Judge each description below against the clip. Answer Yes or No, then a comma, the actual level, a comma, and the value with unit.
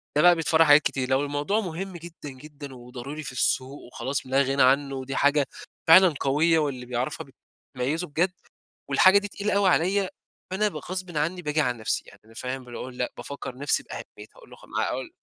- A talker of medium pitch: Yes, medium, 145 Hz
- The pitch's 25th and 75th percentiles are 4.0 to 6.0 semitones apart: Yes, average, 4.6 semitones